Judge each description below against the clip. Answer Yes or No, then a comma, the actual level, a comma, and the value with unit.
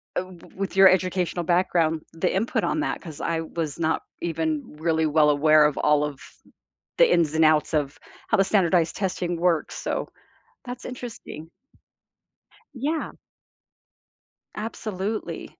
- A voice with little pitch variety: No, average, 3.5 semitones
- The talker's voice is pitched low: No, medium, 170 Hz